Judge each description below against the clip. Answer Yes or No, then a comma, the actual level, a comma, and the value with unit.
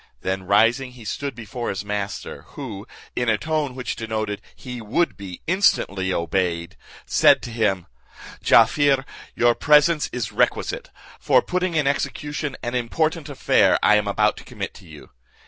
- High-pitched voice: No, low, 120 Hz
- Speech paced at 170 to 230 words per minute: No, average, 155 wpm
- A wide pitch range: Yes, wide, 5.8 semitones